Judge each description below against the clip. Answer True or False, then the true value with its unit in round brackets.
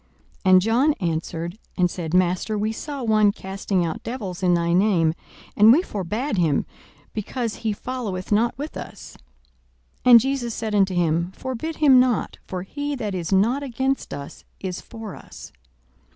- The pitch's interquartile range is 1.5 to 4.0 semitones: False (5.5 semitones)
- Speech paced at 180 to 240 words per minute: False (165 wpm)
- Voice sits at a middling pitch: False (210 Hz)